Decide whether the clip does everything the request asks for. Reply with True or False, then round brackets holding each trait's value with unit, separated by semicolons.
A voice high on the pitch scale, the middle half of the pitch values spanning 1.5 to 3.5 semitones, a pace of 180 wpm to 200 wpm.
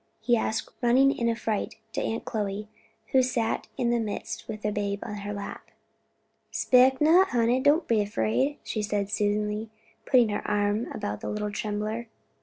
False (220 Hz; 2.7 semitones; 170 wpm)